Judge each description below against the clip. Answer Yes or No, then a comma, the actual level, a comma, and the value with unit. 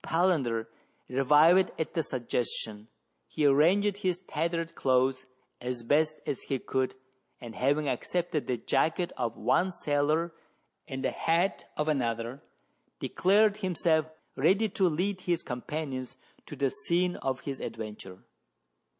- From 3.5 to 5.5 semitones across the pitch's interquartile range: Yes, average, 5.2 semitones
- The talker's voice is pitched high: No, medium, 150 Hz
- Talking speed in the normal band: No, slow, 125 wpm